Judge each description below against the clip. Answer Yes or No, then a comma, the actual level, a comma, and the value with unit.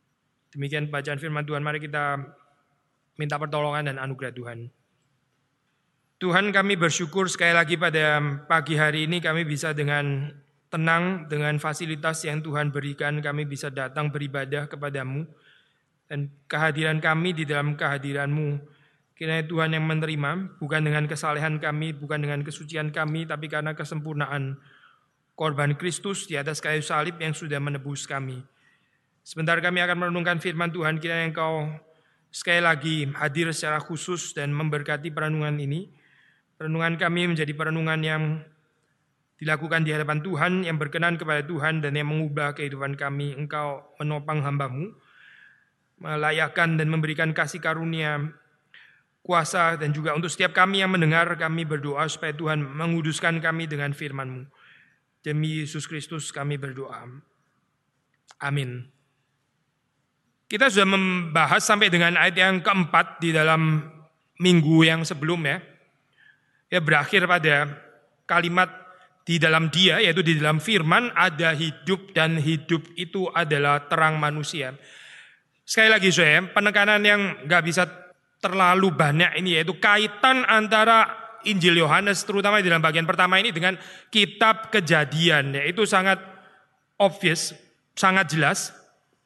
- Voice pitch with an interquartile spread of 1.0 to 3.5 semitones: Yes, average, 2.8 semitones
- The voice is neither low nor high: Yes, medium, 155 Hz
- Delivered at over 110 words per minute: Yes, average, 130 wpm